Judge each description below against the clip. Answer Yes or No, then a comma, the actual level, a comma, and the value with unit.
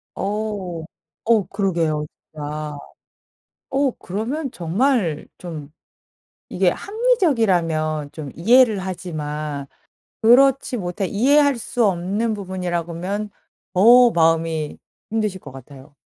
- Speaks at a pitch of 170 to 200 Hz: Yes, medium, 185 Hz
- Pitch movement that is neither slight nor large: No, wide, 6.2 semitones